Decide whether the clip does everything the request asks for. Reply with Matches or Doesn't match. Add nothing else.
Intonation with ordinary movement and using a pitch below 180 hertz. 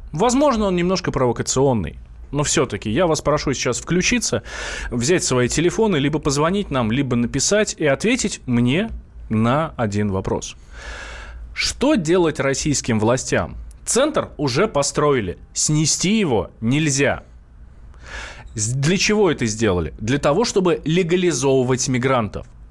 Doesn't match